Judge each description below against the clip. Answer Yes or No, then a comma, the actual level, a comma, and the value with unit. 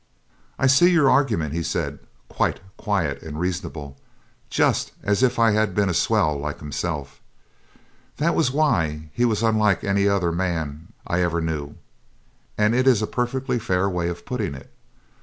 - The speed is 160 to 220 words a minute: Yes, average, 165 wpm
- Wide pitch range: Yes, wide, 6.4 semitones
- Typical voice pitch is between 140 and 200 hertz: No, very low, 95 Hz